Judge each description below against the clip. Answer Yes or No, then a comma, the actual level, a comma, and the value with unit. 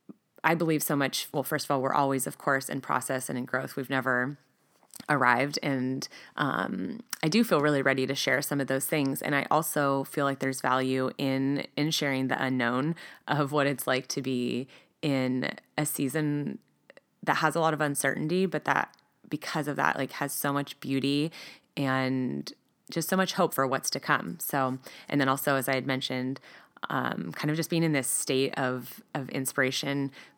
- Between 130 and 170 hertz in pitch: Yes, medium, 140 Hz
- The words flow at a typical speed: Yes, average, 195 wpm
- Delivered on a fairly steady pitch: Yes, narrow, 1.9 semitones